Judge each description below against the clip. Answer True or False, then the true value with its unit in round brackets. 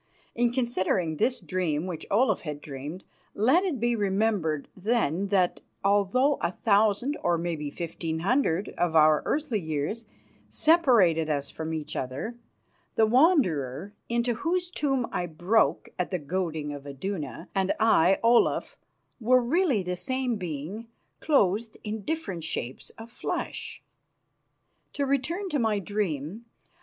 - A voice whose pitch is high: True (200 Hz)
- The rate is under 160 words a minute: True (135 wpm)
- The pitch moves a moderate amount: False (6.8 semitones)